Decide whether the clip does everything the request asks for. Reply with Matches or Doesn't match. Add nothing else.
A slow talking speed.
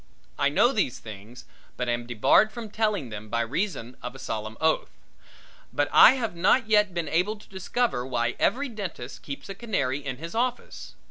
Doesn't match